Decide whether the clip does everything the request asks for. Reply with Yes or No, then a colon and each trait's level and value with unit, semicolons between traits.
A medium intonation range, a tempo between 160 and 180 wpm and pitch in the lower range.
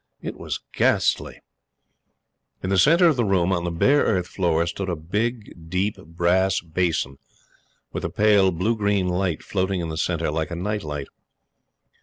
Yes: average, 3.4 semitones; average, 170 wpm; very low, 90 Hz